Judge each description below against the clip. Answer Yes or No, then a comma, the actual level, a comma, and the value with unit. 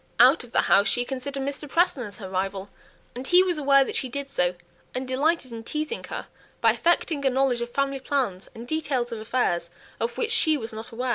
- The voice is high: Yes, very high, 260 Hz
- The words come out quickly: Yes, fast, 215 wpm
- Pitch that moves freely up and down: No, average, 3.8 semitones